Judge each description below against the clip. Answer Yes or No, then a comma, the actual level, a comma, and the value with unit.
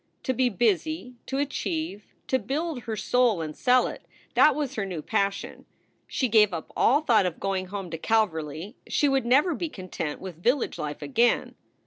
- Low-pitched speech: No, high, 225 Hz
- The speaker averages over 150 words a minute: Yes, average, 180 wpm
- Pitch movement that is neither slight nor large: No, wide, 6.1 semitones